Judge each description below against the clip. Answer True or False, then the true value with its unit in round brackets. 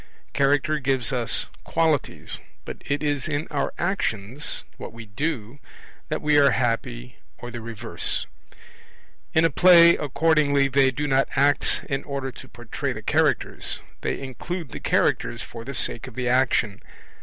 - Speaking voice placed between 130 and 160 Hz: True (135 Hz)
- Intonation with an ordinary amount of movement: True (3.5 semitones)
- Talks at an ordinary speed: True (155 wpm)